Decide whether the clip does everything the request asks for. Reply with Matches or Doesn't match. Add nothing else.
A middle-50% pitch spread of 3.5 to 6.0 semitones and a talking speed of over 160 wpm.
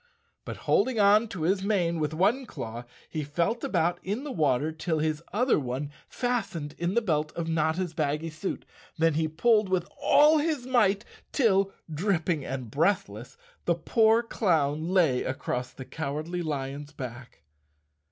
Doesn't match